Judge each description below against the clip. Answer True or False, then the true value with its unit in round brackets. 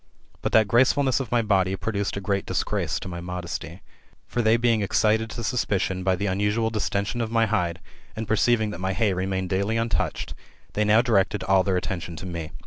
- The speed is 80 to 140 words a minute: False (205 wpm)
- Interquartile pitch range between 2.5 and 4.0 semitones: True (3.2 semitones)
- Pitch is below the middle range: True (100 Hz)